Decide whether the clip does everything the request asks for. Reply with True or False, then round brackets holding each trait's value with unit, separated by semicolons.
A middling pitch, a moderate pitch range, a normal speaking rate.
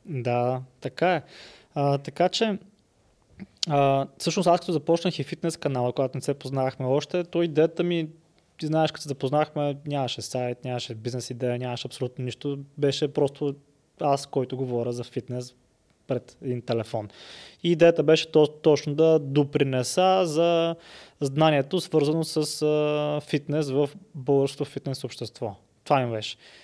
True (145 Hz; 3.7 semitones; 145 wpm)